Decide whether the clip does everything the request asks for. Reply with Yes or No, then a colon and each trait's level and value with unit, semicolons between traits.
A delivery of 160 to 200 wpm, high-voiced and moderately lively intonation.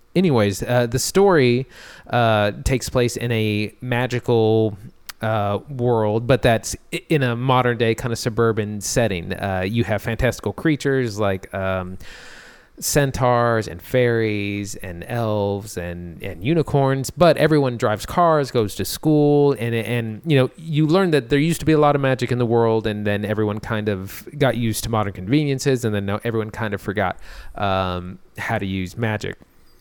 No: average, 165 wpm; low, 115 Hz; average, 4.0 semitones